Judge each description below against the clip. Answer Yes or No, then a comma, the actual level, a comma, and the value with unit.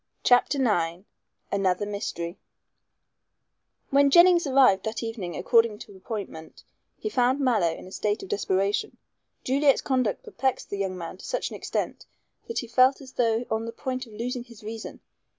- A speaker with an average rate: Yes, average, 165 wpm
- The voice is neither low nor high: No, high, 230 Hz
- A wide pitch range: No, average, 4.6 semitones